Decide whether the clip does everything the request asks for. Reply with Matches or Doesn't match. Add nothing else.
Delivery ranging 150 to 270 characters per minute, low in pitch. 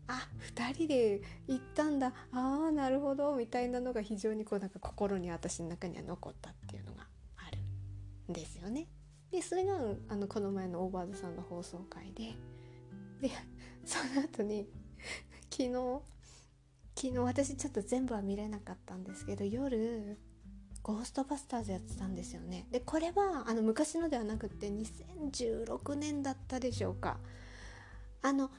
Doesn't match